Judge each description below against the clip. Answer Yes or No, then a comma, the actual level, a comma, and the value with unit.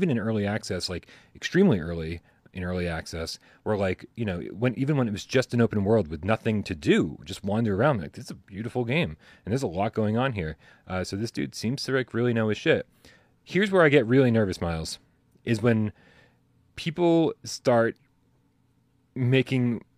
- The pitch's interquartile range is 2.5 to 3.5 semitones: No, average, 4.8 semitones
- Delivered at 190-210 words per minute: Yes, average, 200 wpm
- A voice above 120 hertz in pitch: No, low, 115 Hz